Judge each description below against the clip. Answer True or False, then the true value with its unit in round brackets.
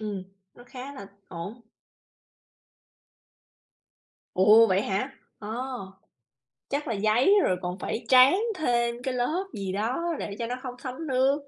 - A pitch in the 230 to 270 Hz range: True (240 Hz)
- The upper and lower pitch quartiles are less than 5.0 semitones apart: True (4.4 semitones)